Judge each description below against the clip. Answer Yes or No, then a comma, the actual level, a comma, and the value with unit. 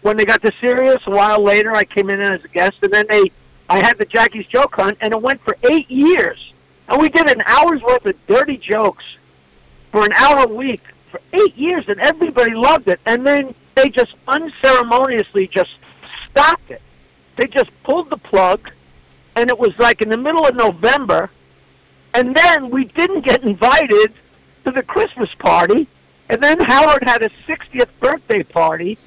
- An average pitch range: No, wide, 6.3 semitones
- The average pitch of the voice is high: Yes, high, 245 Hz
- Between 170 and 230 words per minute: Yes, average, 185 wpm